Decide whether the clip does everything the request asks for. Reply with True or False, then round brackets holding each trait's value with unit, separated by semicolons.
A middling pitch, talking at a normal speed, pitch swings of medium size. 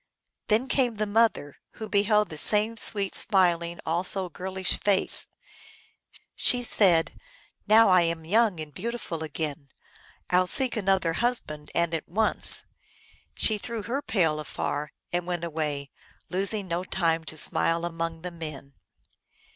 True (180 Hz; 145 wpm; 4.5 semitones)